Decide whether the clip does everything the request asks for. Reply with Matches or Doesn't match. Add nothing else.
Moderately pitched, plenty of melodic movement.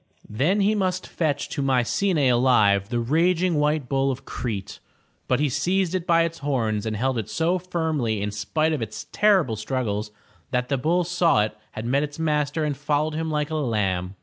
Matches